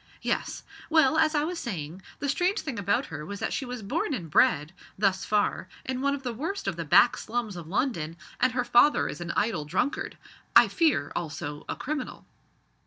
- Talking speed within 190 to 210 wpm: Yes, average, 200 wpm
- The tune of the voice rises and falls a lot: Yes, wide, 8.8 semitones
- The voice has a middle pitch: No, high, 240 Hz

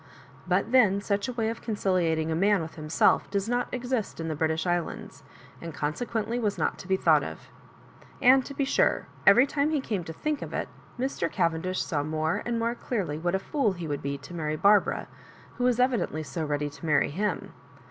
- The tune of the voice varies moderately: No, wide, 6.7 semitones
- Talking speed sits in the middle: No, fast, 210 wpm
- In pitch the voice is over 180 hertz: Yes, high, 190 Hz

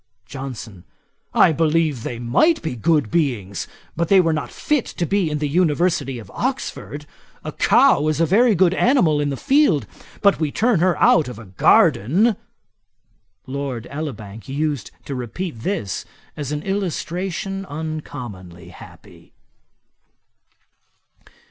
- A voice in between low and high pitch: Yes, medium, 150 Hz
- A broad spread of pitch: Yes, wide, 6.3 semitones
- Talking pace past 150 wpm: No, slow, 135 wpm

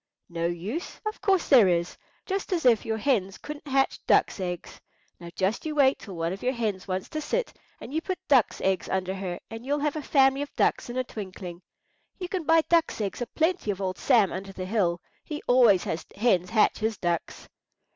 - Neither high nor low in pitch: No, high, 225 Hz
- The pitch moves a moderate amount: No, wide, 7.6 semitones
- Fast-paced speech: Yes, fast, 215 wpm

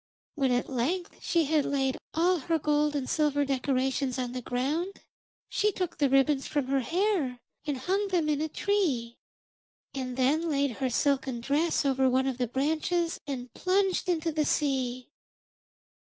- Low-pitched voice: No, very high, 285 Hz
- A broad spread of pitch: No, average, 3.9 semitones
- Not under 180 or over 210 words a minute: No, average, 165 wpm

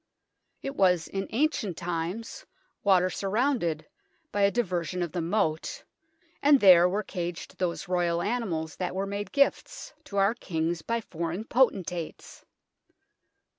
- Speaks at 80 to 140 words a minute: Yes, slow, 135 wpm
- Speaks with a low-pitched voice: No, medium, 185 Hz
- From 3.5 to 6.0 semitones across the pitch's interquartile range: Yes, average, 4.5 semitones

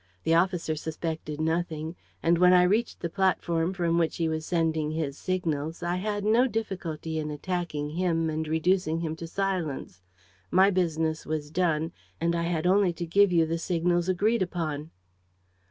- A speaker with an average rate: Yes, average, 170 wpm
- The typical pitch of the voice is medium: Yes, medium, 170 Hz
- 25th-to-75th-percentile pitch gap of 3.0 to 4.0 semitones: No, narrow, 2.4 semitones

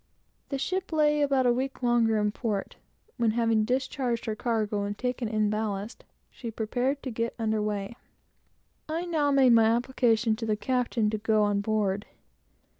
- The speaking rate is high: No, average, 170 wpm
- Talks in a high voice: Yes, high, 230 Hz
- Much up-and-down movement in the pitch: No, average, 3.2 semitones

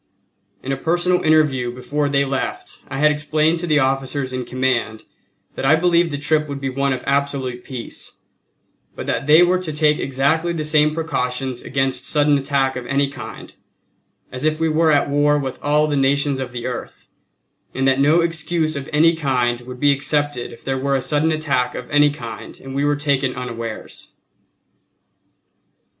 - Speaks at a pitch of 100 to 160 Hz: Yes, medium, 140 Hz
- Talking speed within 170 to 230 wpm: Yes, average, 180 wpm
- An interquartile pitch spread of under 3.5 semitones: Yes, narrow, 2.6 semitones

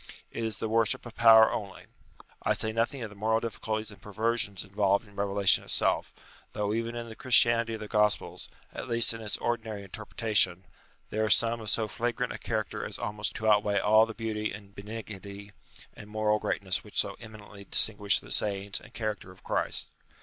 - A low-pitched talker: Yes, low, 110 Hz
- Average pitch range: No, narrow, 1.9 semitones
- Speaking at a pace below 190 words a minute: No, average, 195 wpm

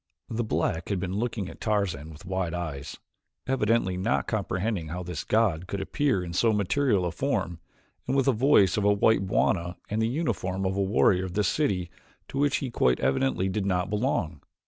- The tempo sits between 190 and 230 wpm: Yes, average, 195 wpm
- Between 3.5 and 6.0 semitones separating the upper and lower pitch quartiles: Yes, average, 4.0 semitones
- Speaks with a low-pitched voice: Yes, very low, 95 Hz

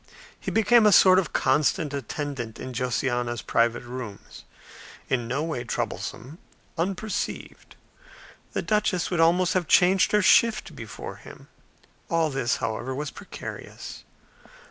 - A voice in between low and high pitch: Yes, medium, 150 Hz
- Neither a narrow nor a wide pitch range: No, wide, 6.9 semitones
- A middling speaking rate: No, slow, 125 wpm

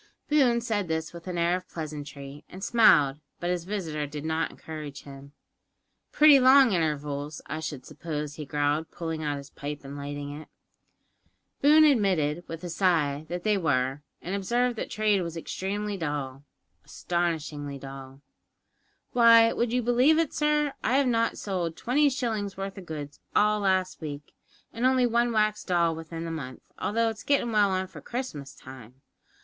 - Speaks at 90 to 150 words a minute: No, average, 170 wpm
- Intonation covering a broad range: Yes, wide, 7.0 semitones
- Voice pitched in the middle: Yes, medium, 170 Hz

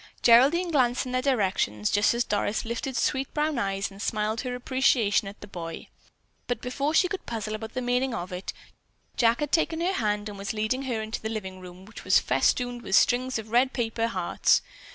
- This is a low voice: No, high, 230 Hz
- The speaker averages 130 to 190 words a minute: No, fast, 205 wpm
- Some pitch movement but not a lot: Yes, average, 3.7 semitones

